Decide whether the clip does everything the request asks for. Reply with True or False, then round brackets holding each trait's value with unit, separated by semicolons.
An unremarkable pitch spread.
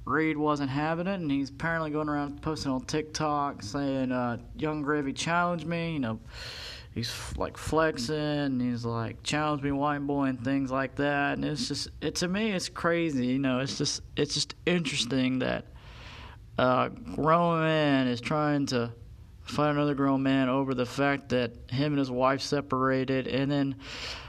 True (3.0 semitones)